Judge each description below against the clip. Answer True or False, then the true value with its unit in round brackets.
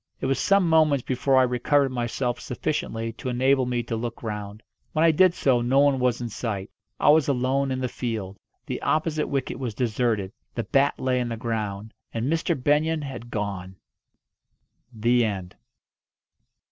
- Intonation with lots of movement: False (3.5 semitones)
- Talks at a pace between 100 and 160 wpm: False (170 wpm)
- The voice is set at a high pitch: False (125 Hz)